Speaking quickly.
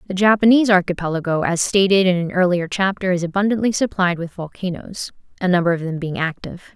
No: average, 180 wpm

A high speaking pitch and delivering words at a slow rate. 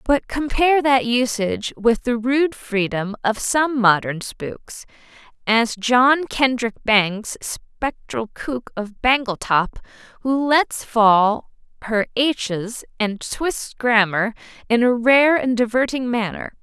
Yes: high, 235 Hz; slow, 125 wpm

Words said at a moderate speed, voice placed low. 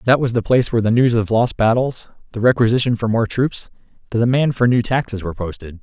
No: fast, 225 wpm; low, 115 Hz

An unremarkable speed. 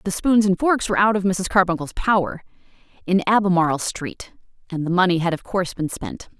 Yes: average, 190 wpm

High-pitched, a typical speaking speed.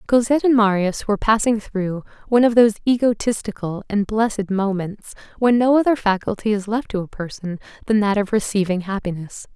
Yes: high, 210 Hz; average, 170 wpm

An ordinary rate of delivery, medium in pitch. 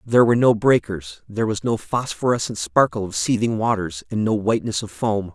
No: average, 190 wpm; low, 110 Hz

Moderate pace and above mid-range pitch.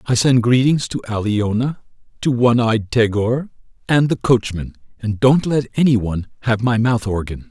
No: average, 170 wpm; low, 120 Hz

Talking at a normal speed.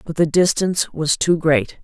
Yes: average, 195 wpm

